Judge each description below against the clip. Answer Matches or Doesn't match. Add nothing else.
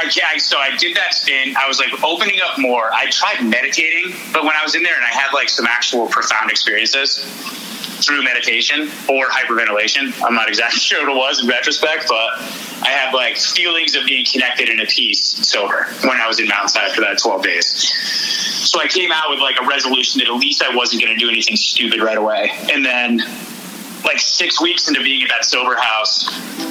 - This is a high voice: Matches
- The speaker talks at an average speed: Doesn't match